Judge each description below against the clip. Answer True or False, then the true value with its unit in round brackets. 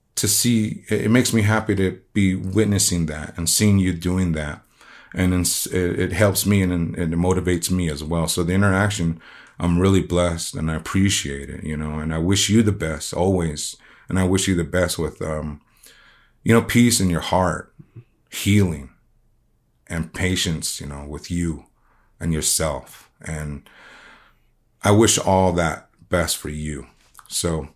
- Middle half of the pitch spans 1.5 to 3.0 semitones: False (3.5 semitones)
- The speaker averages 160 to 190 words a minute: True (165 wpm)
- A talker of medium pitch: False (90 Hz)